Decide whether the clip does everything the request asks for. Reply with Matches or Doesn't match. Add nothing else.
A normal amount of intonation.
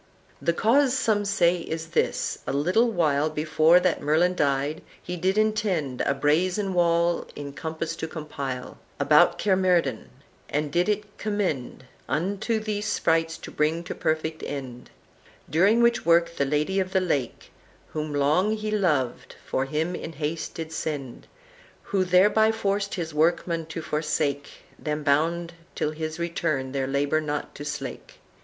Matches